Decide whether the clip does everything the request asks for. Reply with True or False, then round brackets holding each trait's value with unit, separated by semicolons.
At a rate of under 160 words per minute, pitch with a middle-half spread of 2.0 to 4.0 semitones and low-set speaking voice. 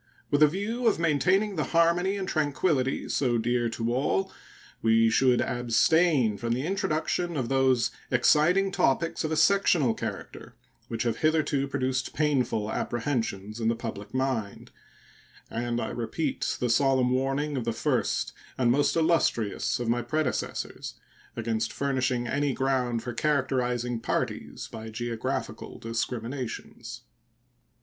False (135 wpm; 4.5 semitones; 130 Hz)